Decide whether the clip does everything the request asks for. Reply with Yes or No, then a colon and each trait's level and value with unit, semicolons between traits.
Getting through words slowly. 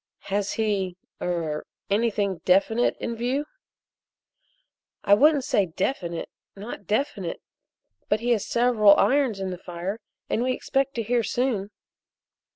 Yes: slow, 130 wpm